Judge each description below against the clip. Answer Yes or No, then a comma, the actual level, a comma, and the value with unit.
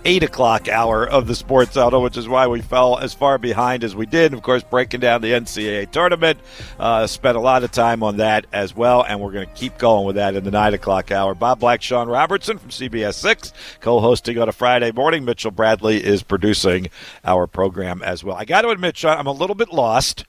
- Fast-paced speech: Yes, fast, 230 wpm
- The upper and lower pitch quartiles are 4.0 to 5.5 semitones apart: No, average, 3.4 semitones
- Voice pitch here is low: Yes, low, 120 Hz